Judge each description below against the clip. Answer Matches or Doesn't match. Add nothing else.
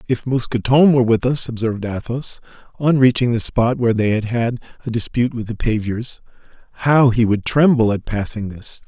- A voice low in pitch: Matches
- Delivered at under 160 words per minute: Doesn't match